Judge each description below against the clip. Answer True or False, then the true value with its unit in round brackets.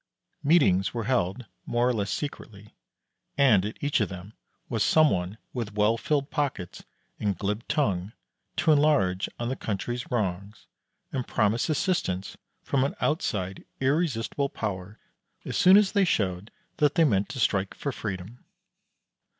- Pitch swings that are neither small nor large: False (6.2 semitones)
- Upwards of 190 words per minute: False (150 wpm)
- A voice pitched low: True (115 Hz)